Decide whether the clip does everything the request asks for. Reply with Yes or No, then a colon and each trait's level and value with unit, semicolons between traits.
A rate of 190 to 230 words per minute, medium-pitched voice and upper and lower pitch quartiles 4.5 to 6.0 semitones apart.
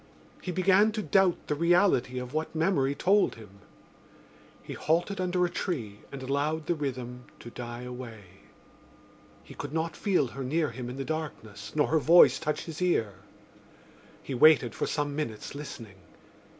No: average, 165 wpm; medium, 150 Hz; wide, 5.4 semitones